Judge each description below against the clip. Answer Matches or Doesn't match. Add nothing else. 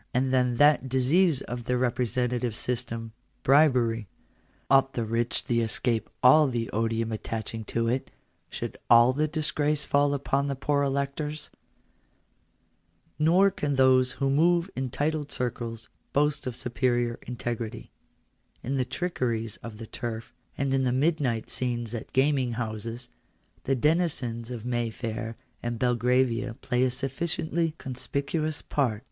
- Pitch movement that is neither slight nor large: Matches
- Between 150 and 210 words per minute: Doesn't match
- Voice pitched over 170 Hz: Doesn't match